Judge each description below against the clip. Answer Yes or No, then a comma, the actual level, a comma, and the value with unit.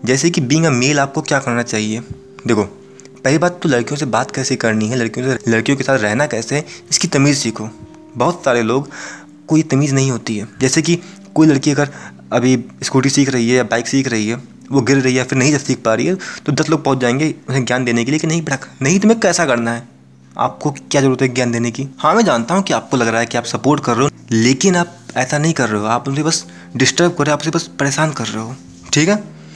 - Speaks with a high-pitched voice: No, low, 135 Hz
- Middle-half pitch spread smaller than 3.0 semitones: No, average, 3.9 semitones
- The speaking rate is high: Yes, fast, 255 wpm